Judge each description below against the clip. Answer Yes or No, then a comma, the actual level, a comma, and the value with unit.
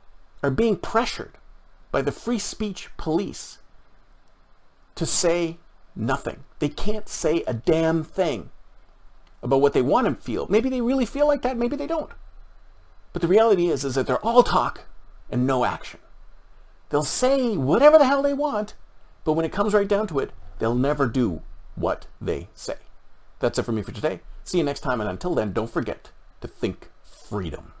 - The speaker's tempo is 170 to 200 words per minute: Yes, average, 180 wpm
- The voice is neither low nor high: Yes, medium, 170 Hz